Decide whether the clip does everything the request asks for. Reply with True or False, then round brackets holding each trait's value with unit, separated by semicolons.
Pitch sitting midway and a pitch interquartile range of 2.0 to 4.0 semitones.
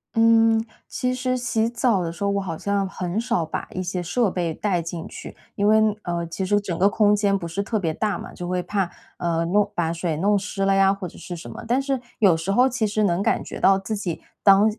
False (195 Hz; 3.6 semitones)